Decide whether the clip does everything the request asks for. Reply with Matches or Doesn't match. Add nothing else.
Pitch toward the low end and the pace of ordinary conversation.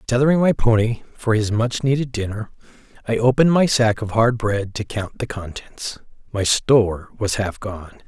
Matches